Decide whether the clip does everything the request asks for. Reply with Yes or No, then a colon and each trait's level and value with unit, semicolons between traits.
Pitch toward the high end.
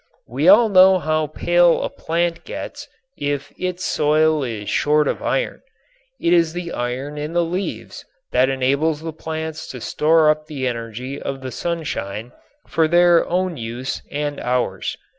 No: medium, 155 Hz